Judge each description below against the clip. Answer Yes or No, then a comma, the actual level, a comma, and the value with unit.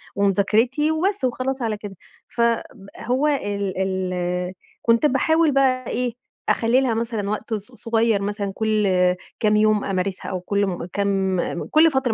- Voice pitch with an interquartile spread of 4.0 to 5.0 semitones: Yes, average, 4.4 semitones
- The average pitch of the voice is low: No, high, 220 Hz